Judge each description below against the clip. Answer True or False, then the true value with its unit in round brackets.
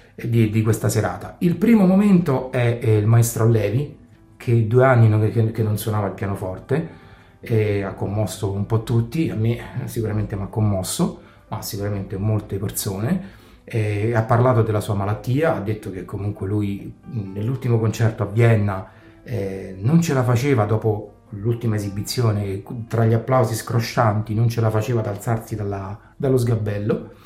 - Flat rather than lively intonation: True (2.3 semitones)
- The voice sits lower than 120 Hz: True (110 Hz)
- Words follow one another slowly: False (165 wpm)